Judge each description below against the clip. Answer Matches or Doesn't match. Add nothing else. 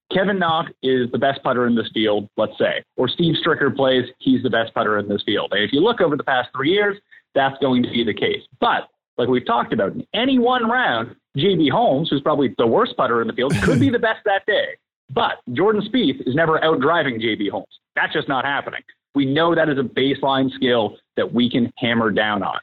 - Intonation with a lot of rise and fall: Matches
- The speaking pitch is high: Doesn't match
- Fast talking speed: Matches